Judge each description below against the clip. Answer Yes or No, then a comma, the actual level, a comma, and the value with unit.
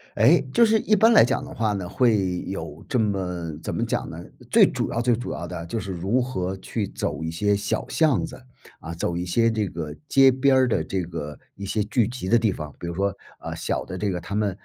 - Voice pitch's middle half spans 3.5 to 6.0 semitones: Yes, average, 5.2 semitones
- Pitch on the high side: No, low, 100 Hz